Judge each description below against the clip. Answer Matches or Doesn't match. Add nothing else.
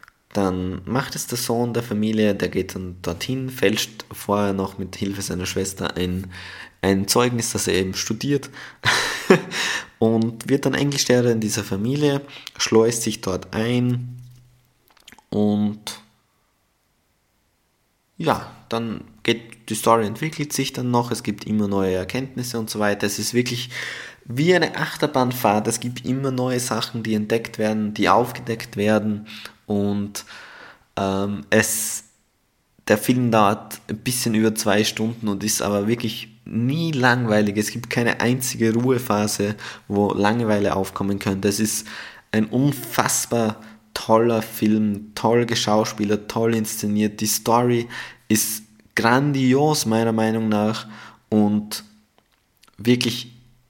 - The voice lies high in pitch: Doesn't match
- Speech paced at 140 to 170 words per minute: Doesn't match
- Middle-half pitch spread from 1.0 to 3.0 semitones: Matches